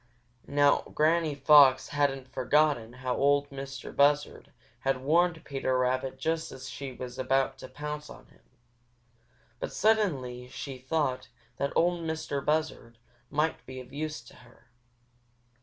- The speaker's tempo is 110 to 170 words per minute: Yes, average, 140 wpm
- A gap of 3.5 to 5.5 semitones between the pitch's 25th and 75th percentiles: No, average, 2.8 semitones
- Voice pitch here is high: No, medium, 140 Hz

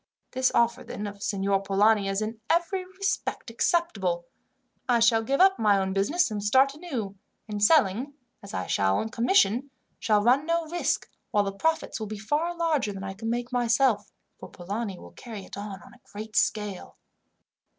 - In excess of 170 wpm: Yes, average, 180 wpm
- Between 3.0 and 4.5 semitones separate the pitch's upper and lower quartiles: No, wide, 5.5 semitones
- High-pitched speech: Yes, high, 225 Hz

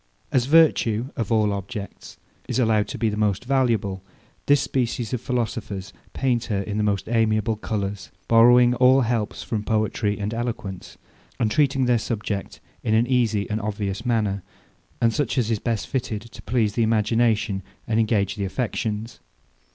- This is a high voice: No, low, 110 Hz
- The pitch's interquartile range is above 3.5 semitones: No, narrow, 2.6 semitones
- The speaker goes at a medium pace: Yes, average, 165 wpm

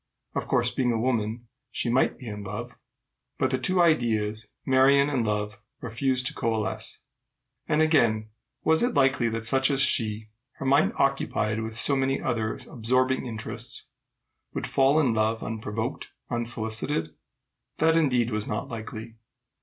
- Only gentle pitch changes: No, average, 3.4 semitones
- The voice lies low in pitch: Yes, low, 120 Hz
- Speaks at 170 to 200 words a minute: No, average, 150 wpm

